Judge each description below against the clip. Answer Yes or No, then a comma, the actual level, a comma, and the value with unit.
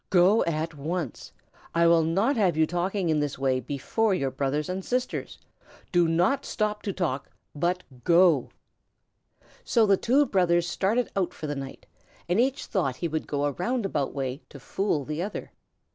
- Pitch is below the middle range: No, medium, 175 Hz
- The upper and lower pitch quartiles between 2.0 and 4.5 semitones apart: No, average, 5.0 semitones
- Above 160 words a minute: Yes, average, 175 wpm